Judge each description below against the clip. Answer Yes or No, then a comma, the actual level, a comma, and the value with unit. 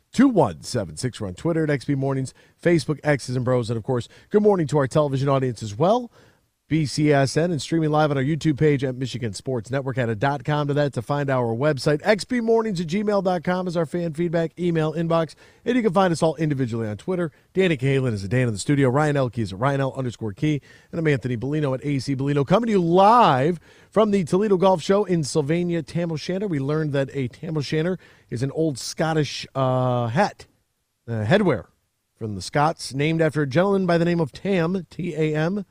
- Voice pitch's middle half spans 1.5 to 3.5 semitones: No, average, 4.4 semitones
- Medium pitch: Yes, medium, 150 Hz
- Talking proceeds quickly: Yes, fast, 210 wpm